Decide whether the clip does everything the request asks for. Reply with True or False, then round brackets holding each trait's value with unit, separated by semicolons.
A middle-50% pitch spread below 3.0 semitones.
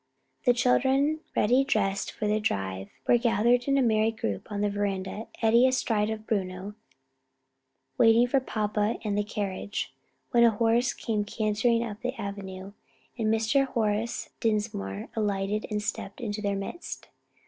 True (2.6 semitones)